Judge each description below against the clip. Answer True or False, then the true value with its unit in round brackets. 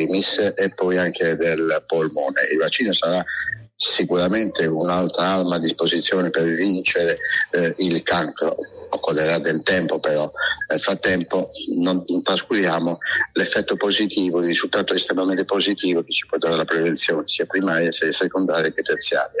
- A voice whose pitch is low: True (90 Hz)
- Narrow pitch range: True (2.2 semitones)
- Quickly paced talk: False (135 wpm)